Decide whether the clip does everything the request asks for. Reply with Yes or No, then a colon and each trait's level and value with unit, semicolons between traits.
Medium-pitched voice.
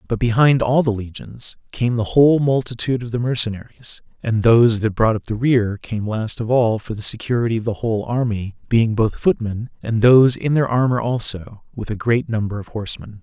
No: low, 115 Hz